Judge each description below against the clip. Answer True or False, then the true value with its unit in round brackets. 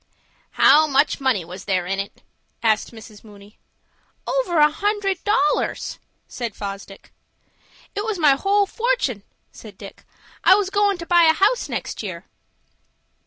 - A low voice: False (300 Hz)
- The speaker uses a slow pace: False (145 wpm)